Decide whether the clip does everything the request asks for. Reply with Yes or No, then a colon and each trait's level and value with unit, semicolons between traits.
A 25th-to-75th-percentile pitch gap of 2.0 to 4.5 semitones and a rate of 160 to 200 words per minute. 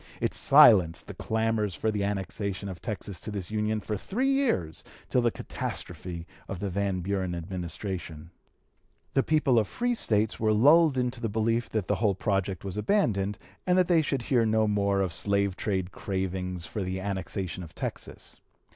Yes: average, 3.2 semitones; average, 180 wpm